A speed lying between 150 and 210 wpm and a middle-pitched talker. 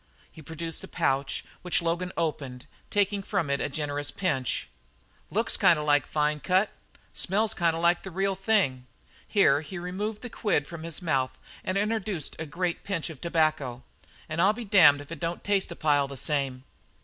Yes: average, 185 wpm; medium, 165 Hz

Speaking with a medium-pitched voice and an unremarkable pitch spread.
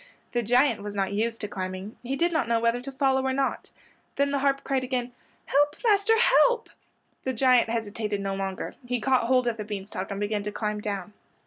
No: high, 235 Hz; average, 4.4 semitones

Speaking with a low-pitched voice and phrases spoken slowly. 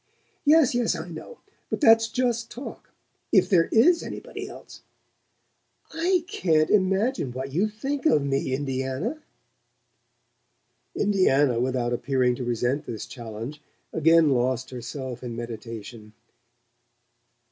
No: medium, 145 Hz; slow, 120 wpm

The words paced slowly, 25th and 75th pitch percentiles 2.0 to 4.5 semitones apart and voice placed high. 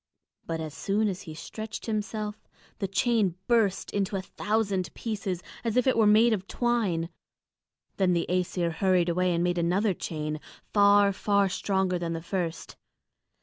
No: average, 160 wpm; average, 3.3 semitones; high, 195 Hz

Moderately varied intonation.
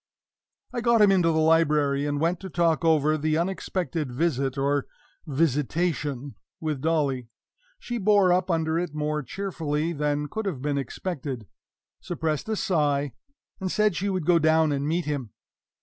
Yes: average, 3.5 semitones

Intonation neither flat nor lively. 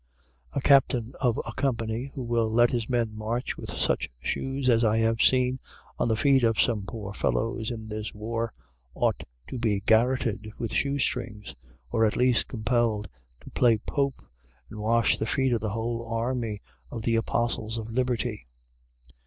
No: narrow, 2.1 semitones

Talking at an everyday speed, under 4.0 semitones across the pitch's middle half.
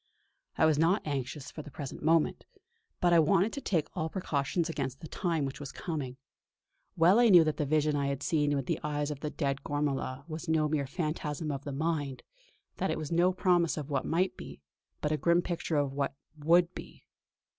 No: fast, 210 wpm; average, 2.8 semitones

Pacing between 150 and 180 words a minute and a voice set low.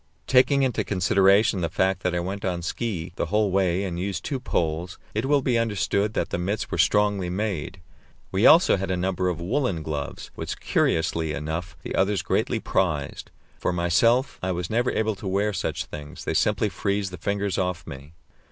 No: average, 190 wpm; very low, 95 Hz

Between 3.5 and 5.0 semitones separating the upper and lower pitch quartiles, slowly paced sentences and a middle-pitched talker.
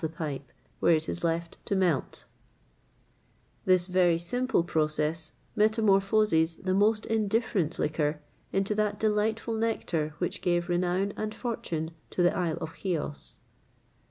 Yes: average, 4.5 semitones; slow, 105 wpm; medium, 180 Hz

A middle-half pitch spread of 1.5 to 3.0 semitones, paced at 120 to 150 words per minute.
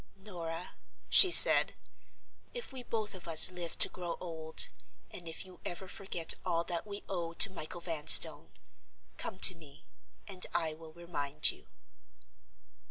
Yes: narrow, 2.5 semitones; average, 145 wpm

